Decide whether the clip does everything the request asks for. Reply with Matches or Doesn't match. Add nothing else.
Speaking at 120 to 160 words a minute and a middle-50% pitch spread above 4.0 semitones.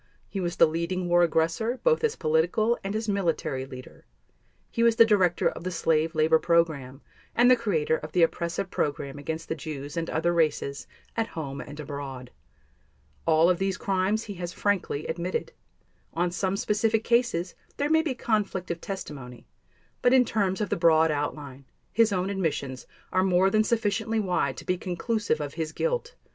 Doesn't match